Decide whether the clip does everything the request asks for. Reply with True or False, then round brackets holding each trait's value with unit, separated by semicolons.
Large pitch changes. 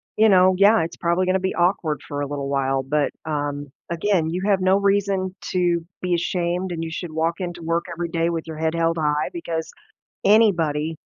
False (2.8 semitones)